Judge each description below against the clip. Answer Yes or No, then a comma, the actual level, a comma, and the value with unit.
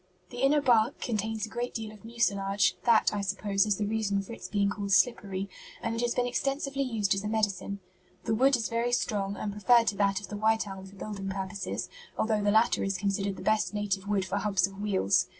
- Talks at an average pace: No, fast, 225 wpm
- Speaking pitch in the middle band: No, high, 210 Hz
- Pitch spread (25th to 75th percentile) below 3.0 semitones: Yes, narrow, 2.5 semitones